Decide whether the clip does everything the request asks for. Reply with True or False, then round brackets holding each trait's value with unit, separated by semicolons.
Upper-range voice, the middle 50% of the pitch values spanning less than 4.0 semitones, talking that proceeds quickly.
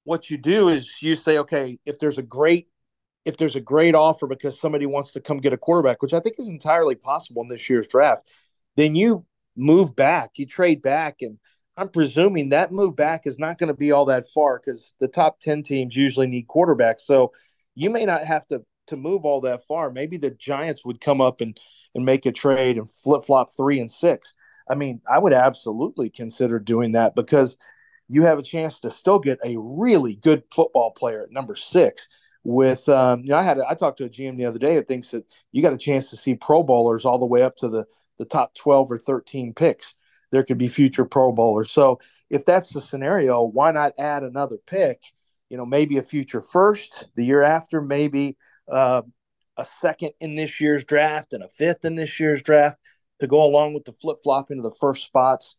False (140 Hz; 3.4 semitones; 220 wpm)